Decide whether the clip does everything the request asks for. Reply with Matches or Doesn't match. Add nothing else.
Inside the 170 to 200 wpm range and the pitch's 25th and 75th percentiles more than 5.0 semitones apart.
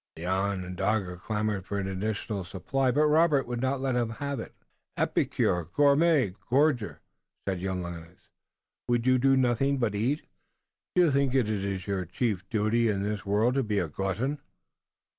Doesn't match